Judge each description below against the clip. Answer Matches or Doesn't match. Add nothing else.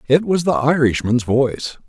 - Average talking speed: Matches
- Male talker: Matches